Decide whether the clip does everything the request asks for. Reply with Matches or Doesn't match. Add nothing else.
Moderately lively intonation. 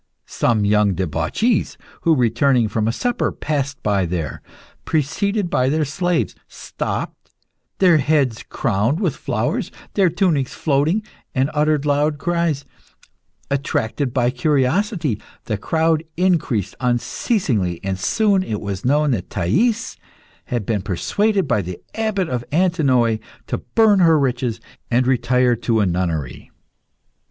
Doesn't match